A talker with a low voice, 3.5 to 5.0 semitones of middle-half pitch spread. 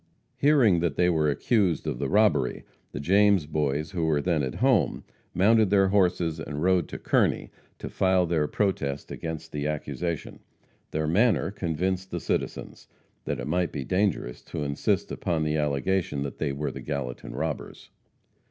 Yes: very low, 80 Hz; average, 4.2 semitones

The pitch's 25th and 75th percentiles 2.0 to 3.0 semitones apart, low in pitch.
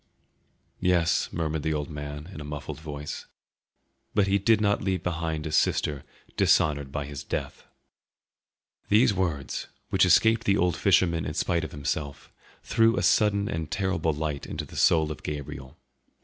No: average, 4.3 semitones; very low, 80 Hz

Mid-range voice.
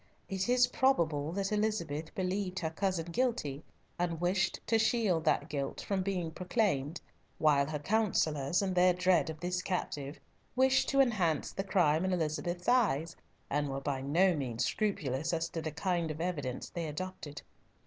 Yes: medium, 175 Hz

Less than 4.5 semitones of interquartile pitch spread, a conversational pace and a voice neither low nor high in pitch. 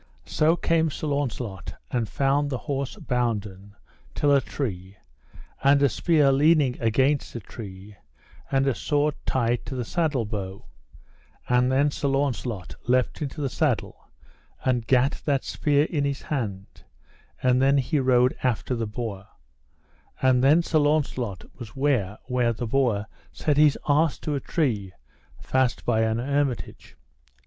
No: average, 3.9 semitones; average, 150 wpm; low, 130 Hz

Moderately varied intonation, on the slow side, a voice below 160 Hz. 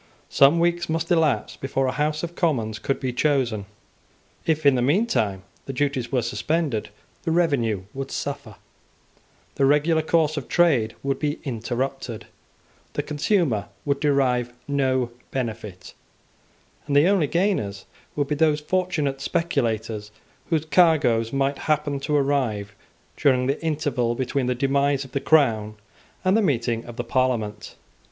No: average, 4.3 semitones; average, 145 wpm; medium, 140 Hz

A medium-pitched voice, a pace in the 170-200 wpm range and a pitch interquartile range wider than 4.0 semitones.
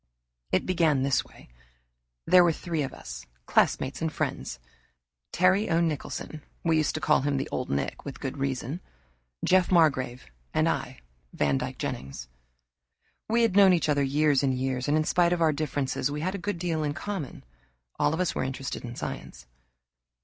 Yes: medium, 150 Hz; average, 180 wpm; average, 4.4 semitones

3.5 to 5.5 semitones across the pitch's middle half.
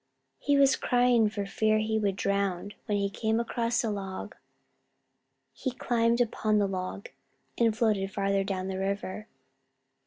No: average, 2.7 semitones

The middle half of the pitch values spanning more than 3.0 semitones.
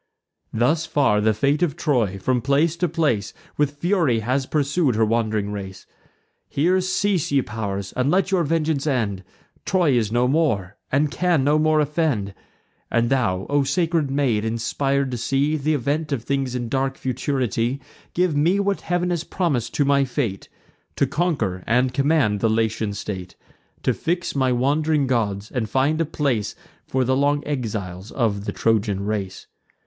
Yes: wide, 5.4 semitones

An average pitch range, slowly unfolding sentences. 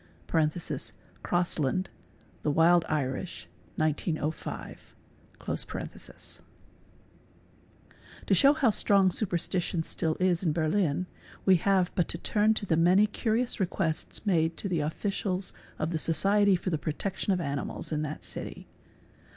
Yes: average, 3.8 semitones; slow, 125 wpm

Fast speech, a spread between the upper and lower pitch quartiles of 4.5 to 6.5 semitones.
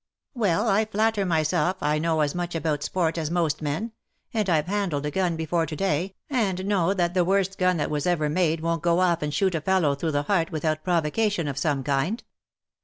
No: fast, 220 wpm; average, 3.7 semitones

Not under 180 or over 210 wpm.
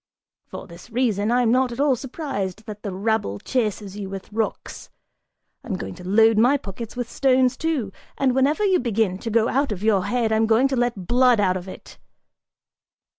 Yes: average, 190 wpm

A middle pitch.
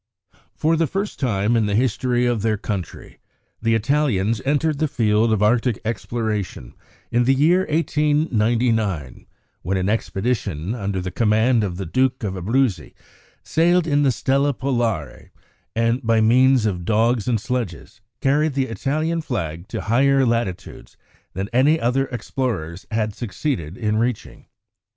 No: low, 115 Hz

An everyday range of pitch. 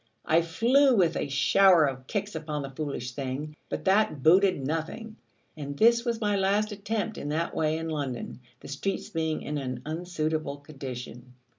No: wide, 5.8 semitones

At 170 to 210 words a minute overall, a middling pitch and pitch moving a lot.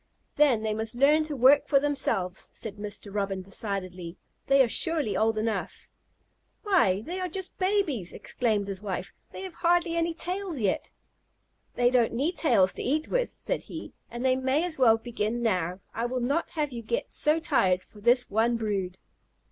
No: average, 180 wpm; high, 240 Hz; wide, 6.7 semitones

